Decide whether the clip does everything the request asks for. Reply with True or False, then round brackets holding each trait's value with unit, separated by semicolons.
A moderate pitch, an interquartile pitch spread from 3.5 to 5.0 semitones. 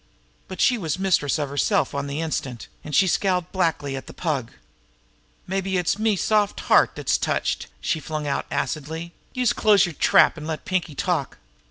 True (165 Hz; 4.5 semitones)